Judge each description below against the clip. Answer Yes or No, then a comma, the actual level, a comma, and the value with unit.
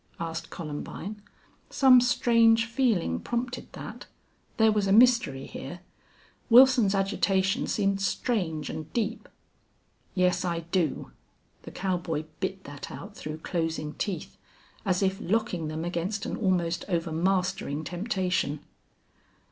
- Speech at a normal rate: No, slow, 115 wpm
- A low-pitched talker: No, high, 190 Hz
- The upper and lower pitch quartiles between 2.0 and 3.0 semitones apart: No, average, 4.5 semitones